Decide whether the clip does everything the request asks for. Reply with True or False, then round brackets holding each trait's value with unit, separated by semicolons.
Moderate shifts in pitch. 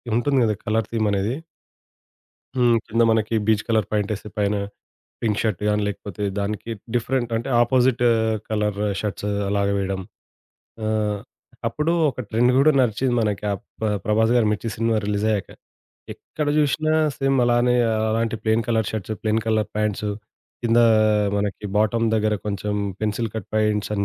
False (2.0 semitones)